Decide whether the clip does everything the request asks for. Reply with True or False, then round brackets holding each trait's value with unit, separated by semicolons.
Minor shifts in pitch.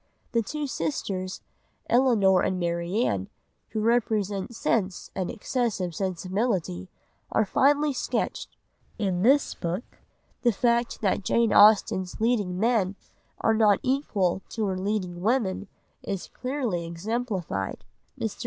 False (4.2 semitones)